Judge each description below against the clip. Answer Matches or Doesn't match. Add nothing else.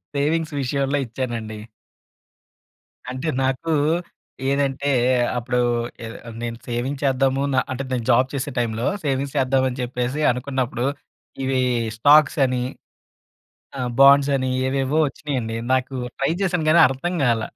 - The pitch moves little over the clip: Matches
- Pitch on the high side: Doesn't match